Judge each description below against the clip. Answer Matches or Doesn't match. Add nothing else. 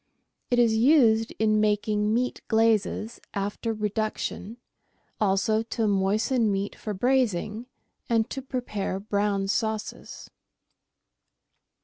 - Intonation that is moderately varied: Doesn't match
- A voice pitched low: Doesn't match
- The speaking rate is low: Matches